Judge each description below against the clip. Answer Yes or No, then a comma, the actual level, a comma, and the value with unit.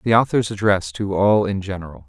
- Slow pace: No, average, 200 wpm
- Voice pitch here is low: Yes, very low, 95 Hz